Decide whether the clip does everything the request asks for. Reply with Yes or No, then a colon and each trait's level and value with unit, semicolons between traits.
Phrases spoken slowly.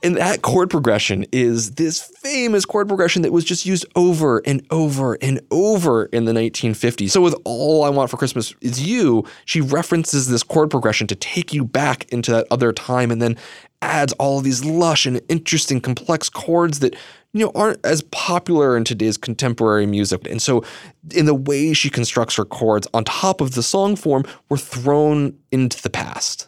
No: average, 190 wpm